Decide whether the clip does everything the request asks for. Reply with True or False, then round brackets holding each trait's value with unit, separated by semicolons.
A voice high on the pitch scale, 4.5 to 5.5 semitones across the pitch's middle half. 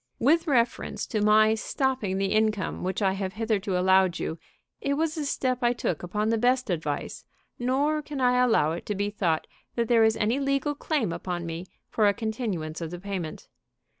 True (215 Hz; 5.1 semitones)